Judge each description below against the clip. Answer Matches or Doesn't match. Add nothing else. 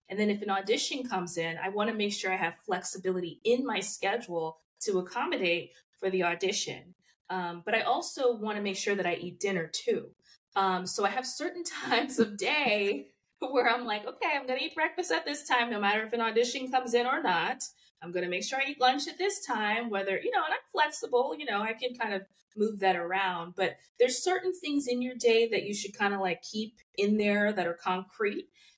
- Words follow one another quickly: Matches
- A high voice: Matches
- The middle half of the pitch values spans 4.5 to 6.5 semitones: Matches